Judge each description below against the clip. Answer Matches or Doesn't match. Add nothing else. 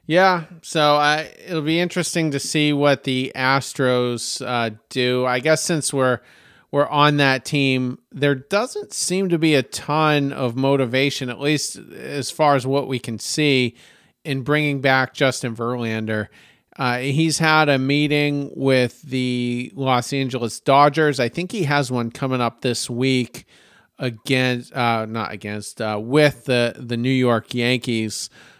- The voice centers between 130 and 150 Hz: Matches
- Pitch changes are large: Doesn't match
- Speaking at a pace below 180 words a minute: Matches